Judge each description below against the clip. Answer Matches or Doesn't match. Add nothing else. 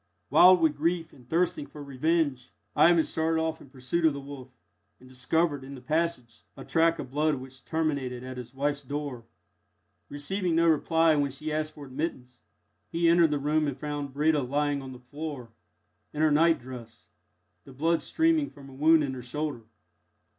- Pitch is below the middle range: Doesn't match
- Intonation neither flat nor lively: Matches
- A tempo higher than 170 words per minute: Matches